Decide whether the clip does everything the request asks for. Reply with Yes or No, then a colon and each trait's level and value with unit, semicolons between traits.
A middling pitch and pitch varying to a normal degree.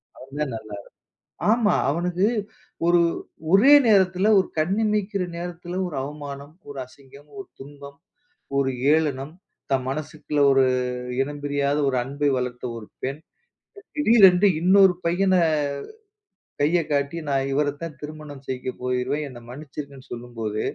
Yes: medium, 145 Hz; average, 4.7 semitones